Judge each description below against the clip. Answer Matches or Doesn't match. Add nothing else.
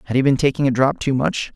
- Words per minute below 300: Doesn't match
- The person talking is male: Matches